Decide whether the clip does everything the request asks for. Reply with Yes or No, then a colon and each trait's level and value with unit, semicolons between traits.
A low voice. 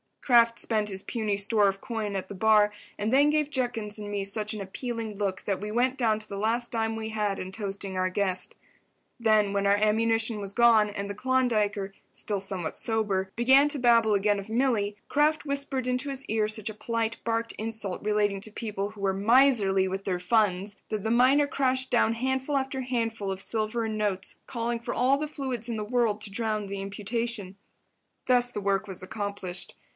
No: high, 215 Hz